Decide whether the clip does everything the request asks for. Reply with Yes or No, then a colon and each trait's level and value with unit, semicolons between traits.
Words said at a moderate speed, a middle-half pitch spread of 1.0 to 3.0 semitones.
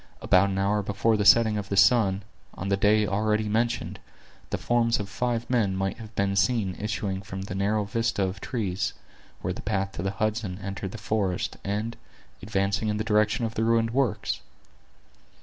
Yes: average, 185 wpm; narrow, 2.4 semitones